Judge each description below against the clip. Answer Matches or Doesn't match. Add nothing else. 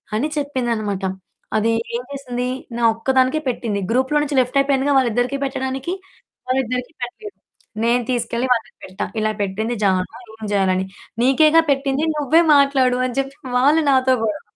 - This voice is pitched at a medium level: Doesn't match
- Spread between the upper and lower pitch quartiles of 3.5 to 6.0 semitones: Doesn't match